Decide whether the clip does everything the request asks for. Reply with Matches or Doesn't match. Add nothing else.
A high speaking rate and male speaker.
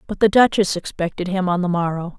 Doesn't match